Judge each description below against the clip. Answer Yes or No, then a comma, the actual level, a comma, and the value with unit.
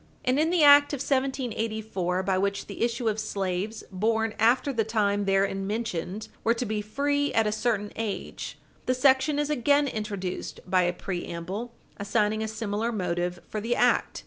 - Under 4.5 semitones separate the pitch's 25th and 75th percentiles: Yes, average, 3.7 semitones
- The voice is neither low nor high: No, high, 220 Hz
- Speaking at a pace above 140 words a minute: Yes, average, 170 wpm